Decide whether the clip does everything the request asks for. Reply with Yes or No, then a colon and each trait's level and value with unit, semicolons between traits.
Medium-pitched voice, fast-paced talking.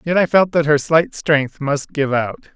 Yes: medium, 150 Hz; fast, 235 wpm